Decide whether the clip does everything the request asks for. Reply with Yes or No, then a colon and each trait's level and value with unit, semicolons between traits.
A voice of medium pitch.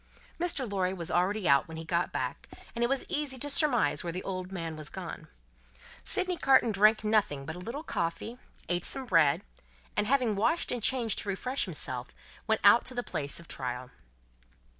No: high, 200 Hz